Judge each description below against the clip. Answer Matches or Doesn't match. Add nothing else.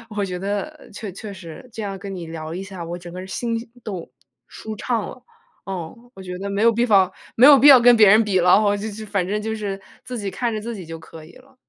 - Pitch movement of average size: Matches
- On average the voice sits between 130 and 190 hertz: Doesn't match